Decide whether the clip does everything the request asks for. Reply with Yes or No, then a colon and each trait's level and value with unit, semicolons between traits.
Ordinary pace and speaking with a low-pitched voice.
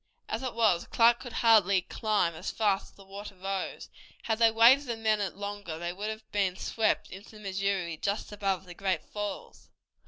No: average, 190 wpm; high, 205 Hz